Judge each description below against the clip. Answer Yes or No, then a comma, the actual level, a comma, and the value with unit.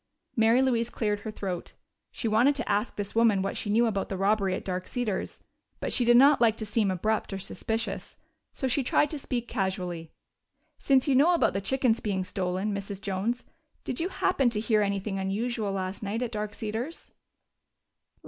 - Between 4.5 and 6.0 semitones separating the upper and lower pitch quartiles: No, average, 3.6 semitones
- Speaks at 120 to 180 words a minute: No, average, 190 wpm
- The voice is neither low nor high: No, high, 215 Hz